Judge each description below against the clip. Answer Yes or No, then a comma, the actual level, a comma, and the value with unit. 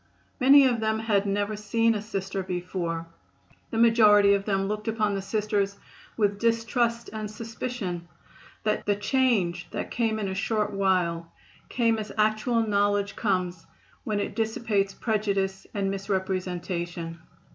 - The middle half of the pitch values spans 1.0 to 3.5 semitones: Yes, narrow, 2.4 semitones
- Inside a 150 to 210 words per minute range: No, slow, 135 wpm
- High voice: Yes, high, 205 Hz